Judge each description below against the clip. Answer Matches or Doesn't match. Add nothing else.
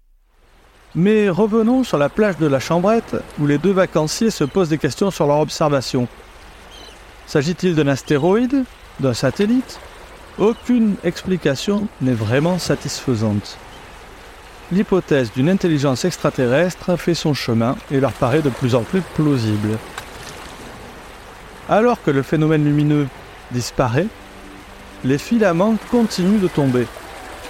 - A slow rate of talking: Matches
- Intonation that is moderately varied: Doesn't match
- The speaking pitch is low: Doesn't match